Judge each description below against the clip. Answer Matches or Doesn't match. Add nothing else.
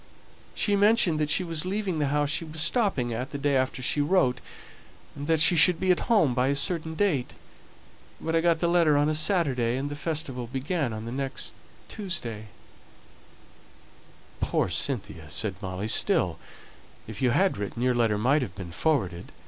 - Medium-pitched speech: Matches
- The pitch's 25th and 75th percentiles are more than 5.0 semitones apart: Matches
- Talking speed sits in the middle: Matches